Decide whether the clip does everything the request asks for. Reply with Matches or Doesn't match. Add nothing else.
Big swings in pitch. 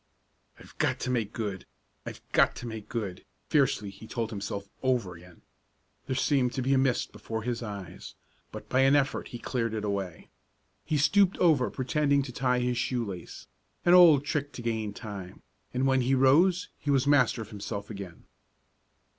Doesn't match